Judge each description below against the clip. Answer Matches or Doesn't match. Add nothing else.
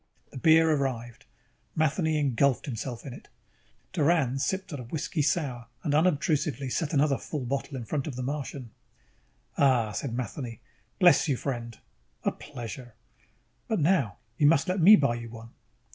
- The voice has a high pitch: Doesn't match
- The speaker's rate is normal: Matches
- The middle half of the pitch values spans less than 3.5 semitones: Doesn't match